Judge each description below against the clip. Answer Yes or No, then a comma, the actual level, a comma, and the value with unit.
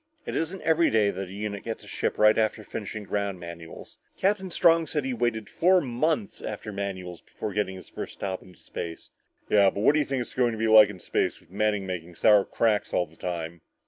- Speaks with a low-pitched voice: Yes, low, 105 Hz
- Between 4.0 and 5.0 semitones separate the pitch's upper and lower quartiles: Yes, average, 4.6 semitones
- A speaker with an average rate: No, fast, 235 wpm